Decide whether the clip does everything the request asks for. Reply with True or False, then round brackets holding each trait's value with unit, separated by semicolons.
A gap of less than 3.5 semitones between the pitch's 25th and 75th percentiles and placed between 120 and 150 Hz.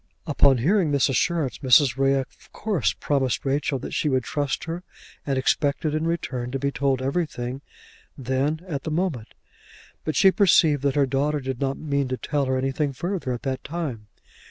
True (2.8 semitones; 140 Hz)